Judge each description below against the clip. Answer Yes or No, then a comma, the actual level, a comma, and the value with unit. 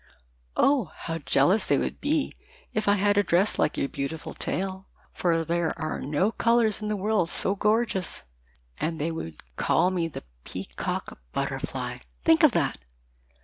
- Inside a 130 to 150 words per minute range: No, average, 160 wpm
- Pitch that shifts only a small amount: No, average, 4.5 semitones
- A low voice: No, medium, 185 Hz